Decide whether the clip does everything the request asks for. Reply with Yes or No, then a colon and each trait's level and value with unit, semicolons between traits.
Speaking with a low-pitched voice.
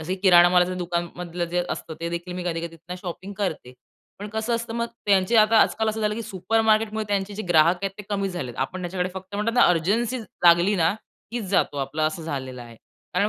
No: medium, 185 Hz